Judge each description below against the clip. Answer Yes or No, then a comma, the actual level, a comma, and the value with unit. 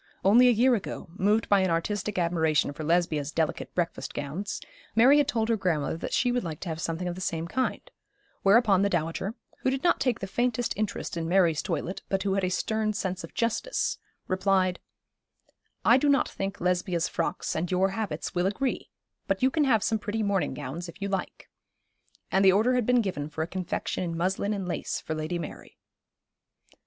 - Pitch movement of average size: Yes, average, 4.5 semitones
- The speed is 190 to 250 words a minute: Yes, average, 200 wpm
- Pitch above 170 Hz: Yes, high, 190 Hz